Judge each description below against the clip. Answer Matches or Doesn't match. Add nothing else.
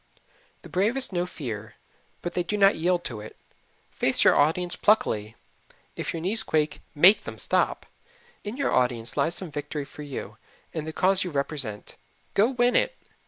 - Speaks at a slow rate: Doesn't match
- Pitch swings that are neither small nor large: Doesn't match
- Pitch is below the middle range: Doesn't match